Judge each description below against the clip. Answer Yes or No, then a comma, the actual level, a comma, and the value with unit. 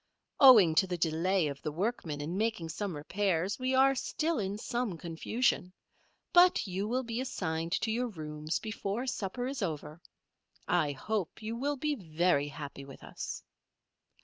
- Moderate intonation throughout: No, wide, 6.8 semitones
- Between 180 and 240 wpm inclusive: No, average, 160 wpm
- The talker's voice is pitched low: No, high, 190 Hz